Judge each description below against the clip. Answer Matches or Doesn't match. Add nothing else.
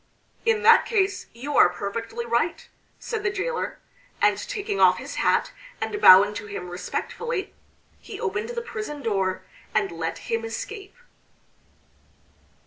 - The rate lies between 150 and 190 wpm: Doesn't match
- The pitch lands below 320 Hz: Doesn't match